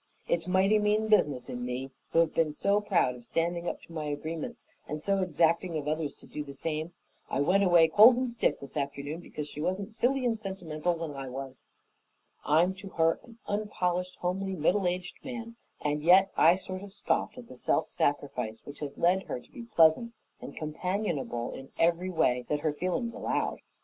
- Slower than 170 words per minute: No, average, 195 wpm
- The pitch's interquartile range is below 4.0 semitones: No, average, 4.6 semitones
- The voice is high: No, medium, 170 Hz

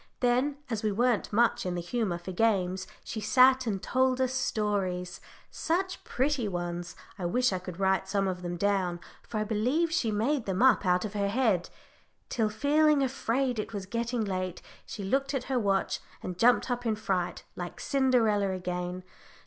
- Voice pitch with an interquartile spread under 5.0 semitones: No, average, 5.3 semitones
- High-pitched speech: Yes, high, 215 Hz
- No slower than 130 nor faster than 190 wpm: Yes, average, 185 wpm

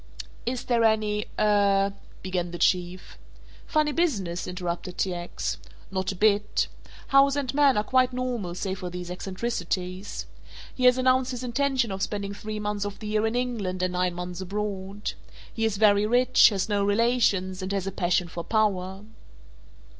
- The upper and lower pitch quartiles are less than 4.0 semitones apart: No, average, 4.3 semitones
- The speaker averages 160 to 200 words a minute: Yes, average, 170 wpm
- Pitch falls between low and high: No, high, 205 Hz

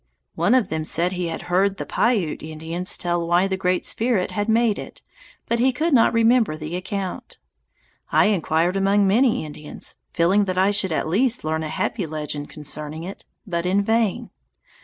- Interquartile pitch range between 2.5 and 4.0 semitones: No, average, 4.4 semitones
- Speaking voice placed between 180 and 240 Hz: Yes, medium, 185 Hz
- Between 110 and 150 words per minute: No, average, 180 wpm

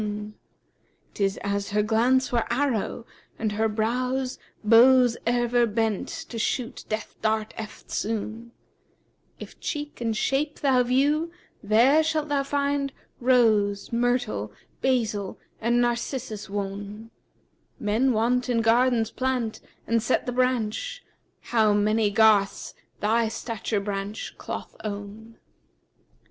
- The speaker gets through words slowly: Yes, slow, 125 wpm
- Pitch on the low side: No, high, 230 Hz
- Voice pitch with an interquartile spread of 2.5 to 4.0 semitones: Yes, average, 3.0 semitones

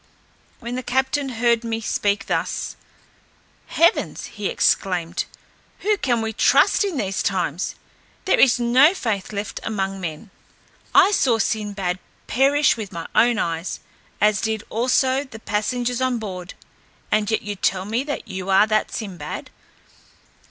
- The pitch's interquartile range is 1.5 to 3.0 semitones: No, average, 4.2 semitones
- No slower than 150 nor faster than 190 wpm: No, average, 140 wpm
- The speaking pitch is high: Yes, high, 220 Hz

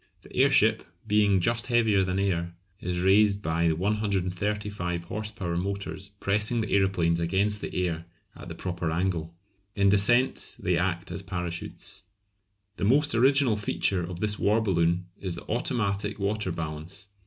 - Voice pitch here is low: Yes, very low, 95 Hz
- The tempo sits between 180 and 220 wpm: No, average, 155 wpm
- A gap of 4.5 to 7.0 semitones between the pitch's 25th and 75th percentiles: No, average, 3.3 semitones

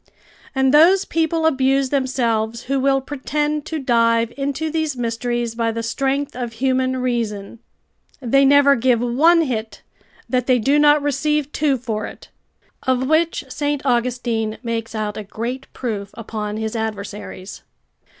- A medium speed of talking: Yes, average, 145 wpm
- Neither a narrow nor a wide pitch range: Yes, average, 3.6 semitones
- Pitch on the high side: Yes, very high, 255 Hz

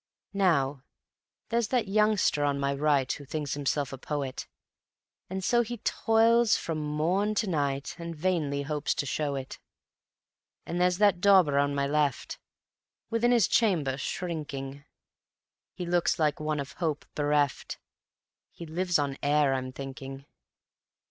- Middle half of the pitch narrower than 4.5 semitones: No, average, 4.8 semitones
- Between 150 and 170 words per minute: No, average, 140 wpm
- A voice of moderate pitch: Yes, medium, 150 Hz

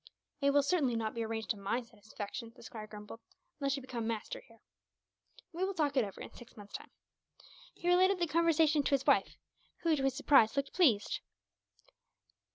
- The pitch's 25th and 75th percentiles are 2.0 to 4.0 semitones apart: No, average, 5.3 semitones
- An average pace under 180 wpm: No, average, 185 wpm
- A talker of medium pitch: No, very high, 265 Hz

